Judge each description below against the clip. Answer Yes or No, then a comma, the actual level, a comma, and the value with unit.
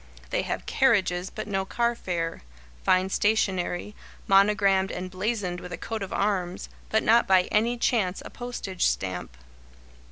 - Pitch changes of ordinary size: Yes, average, 3.2 semitones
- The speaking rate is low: No, average, 150 wpm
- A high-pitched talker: Yes, high, 195 Hz